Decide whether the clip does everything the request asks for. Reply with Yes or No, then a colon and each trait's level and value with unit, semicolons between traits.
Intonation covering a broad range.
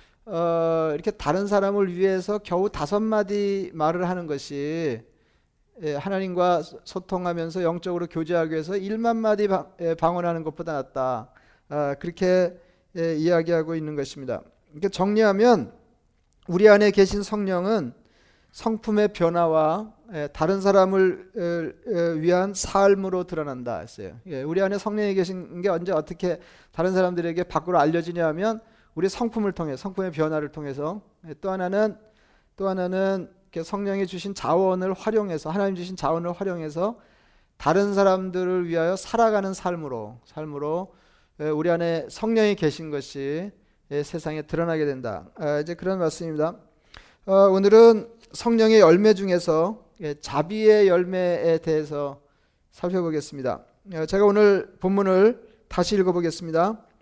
No: average, 3.7 semitones